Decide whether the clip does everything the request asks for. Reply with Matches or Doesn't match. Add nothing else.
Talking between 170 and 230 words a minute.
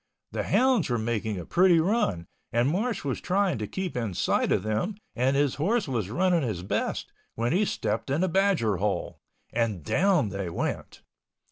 Matches